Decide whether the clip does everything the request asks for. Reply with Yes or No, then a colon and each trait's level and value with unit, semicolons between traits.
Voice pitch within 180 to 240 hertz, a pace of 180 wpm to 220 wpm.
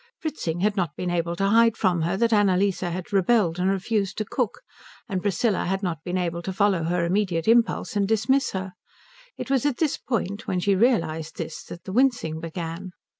Yes: high, 190 Hz; average, 200 wpm